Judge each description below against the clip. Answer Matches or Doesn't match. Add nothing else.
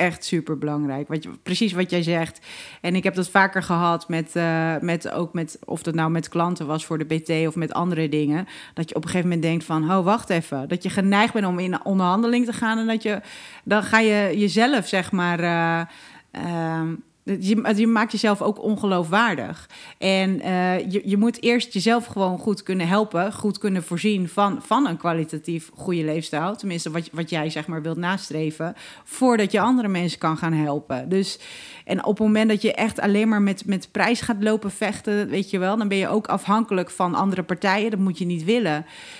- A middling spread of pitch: Matches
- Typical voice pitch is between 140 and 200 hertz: Matches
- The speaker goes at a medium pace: Doesn't match